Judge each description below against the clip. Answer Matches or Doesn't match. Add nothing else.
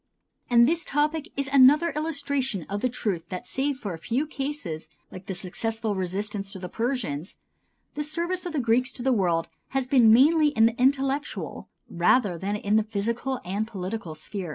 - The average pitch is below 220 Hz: Doesn't match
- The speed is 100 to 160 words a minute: Doesn't match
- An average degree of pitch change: Doesn't match